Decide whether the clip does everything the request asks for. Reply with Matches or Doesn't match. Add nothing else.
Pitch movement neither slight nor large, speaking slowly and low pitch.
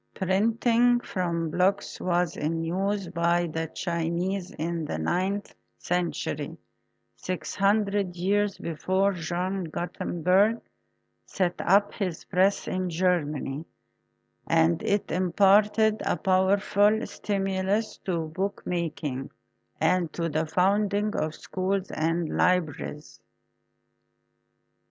Doesn't match